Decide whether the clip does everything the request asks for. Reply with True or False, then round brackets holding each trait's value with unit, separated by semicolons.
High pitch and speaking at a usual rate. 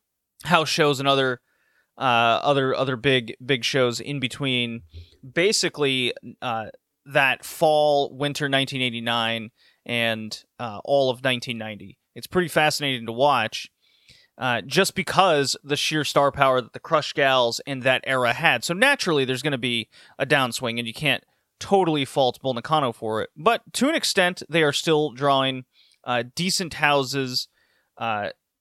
False (135 Hz; 145 wpm)